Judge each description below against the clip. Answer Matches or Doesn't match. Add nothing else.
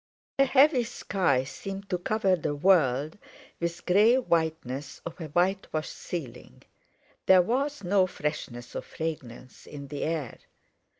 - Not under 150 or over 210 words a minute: Doesn't match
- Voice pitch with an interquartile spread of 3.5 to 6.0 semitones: Matches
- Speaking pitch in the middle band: Matches